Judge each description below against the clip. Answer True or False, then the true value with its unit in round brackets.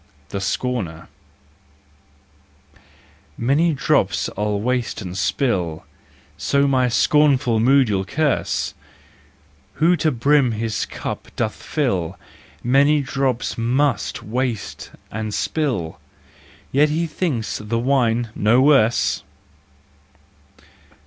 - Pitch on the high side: False (125 Hz)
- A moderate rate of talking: False (95 wpm)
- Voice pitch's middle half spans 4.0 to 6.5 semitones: True (4.6 semitones)